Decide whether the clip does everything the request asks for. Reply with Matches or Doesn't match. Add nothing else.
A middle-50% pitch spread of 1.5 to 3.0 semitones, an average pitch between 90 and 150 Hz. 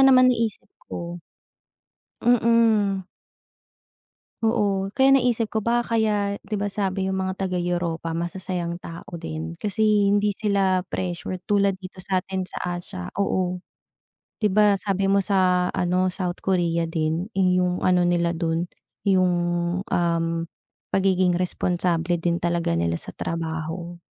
Doesn't match